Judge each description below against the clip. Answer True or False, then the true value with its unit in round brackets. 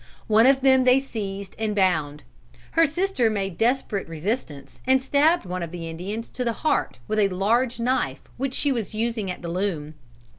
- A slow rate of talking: False (185 wpm)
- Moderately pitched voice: False (215 Hz)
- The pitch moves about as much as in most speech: False (6.1 semitones)